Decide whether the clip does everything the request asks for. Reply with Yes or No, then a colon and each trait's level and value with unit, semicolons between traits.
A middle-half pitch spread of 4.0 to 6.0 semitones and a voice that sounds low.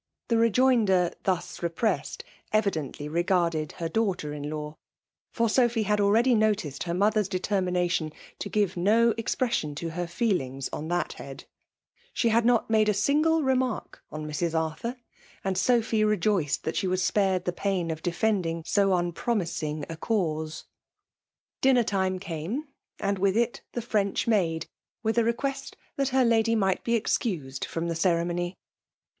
No: average, 5.2 semitones; high, 195 Hz